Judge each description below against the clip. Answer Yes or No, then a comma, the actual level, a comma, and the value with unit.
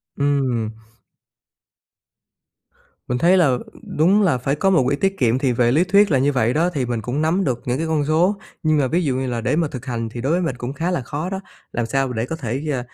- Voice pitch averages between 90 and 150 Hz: Yes, medium, 140 Hz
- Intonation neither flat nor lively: Yes, average, 4.7 semitones